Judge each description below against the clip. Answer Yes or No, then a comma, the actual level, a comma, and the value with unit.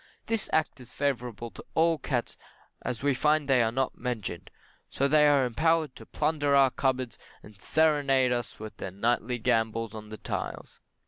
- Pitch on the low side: Yes, low, 130 Hz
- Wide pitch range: No, average, 4.1 semitones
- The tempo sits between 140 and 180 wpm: Yes, average, 175 wpm